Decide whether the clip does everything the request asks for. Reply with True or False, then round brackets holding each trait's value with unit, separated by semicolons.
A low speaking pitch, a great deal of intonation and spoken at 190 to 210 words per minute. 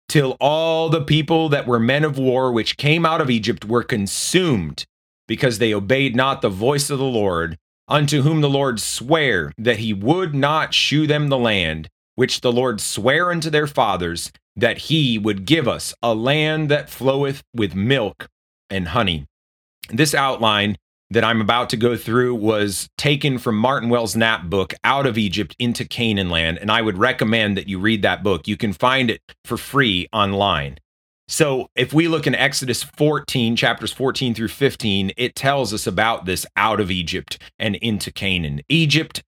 False (115 Hz; 5.7 semitones; 180 wpm)